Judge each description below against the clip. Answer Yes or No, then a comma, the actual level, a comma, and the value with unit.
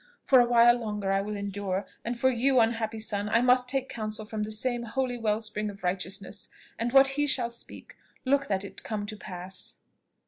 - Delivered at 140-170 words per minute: No, fast, 205 wpm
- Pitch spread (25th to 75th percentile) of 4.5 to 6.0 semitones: No, average, 3.1 semitones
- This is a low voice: No, high, 220 Hz